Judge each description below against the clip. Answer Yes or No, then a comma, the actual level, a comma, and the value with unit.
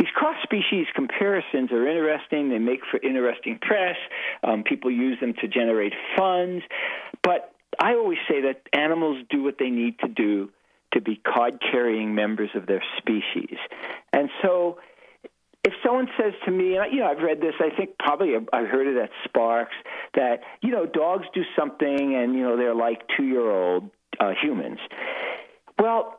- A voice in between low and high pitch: Yes, medium, 145 Hz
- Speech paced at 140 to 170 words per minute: Yes, average, 165 wpm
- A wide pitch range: Yes, wide, 8.9 semitones